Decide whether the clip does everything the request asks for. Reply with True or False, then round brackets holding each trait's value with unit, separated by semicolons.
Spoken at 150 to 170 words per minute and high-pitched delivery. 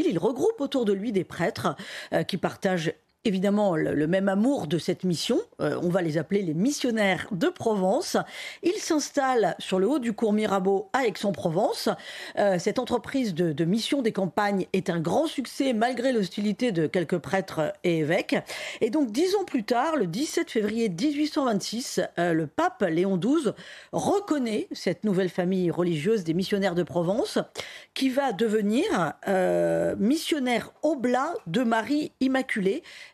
True (160 wpm; 210 Hz)